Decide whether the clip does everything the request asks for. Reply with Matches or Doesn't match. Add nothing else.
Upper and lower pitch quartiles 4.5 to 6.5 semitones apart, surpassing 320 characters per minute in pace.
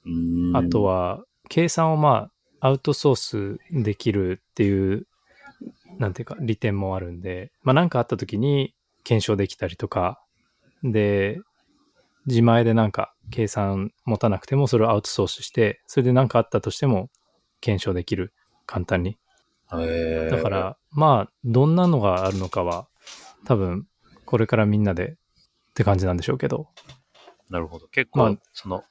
Doesn't match